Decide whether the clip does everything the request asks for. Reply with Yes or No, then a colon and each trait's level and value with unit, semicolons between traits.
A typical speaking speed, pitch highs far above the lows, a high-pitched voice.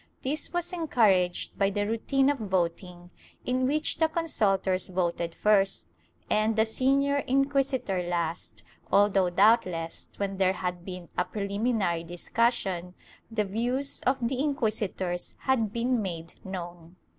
No: slow, 130 wpm; wide, 5.9 semitones; high, 205 Hz